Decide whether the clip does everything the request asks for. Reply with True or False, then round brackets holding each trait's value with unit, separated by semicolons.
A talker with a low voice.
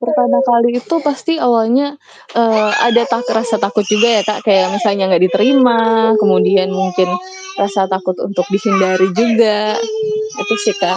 False (215 Hz)